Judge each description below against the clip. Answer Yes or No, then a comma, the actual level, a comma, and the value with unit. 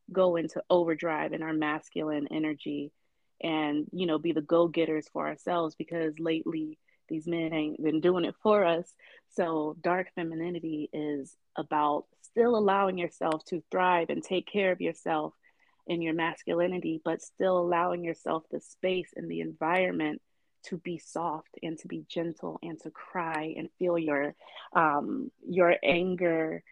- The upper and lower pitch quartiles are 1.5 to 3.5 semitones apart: Yes, narrow, 2.4 semitones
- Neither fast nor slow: Yes, average, 155 wpm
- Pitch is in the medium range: Yes, medium, 165 Hz